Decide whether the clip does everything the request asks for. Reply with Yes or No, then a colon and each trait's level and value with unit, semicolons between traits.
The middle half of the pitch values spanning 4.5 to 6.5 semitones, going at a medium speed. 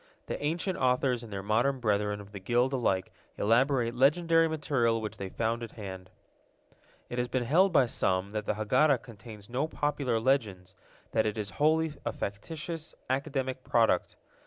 Yes: average, 4.8 semitones; average, 165 wpm